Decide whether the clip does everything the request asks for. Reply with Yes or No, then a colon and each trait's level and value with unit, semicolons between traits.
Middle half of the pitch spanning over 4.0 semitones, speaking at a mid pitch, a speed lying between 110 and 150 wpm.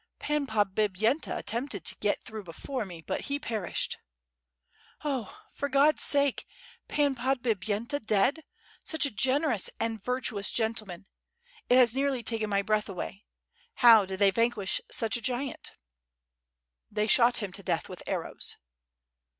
No: average, 4.6 semitones; high, 230 Hz; average, 140 wpm